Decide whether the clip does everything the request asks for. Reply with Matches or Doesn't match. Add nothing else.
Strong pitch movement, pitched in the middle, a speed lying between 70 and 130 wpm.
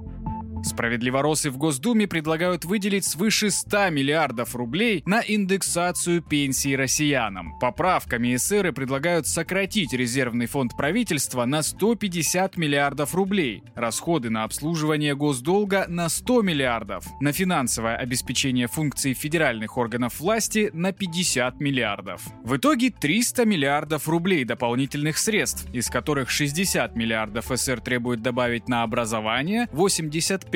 Matches